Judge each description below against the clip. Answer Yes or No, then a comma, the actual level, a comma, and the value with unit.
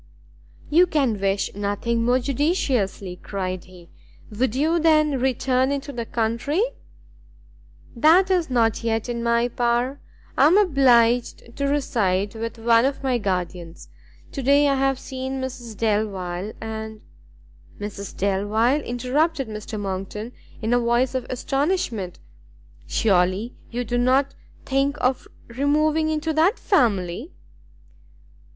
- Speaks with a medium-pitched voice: No, high, 240 Hz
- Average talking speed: No, slow, 130 wpm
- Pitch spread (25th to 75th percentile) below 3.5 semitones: No, average, 4.6 semitones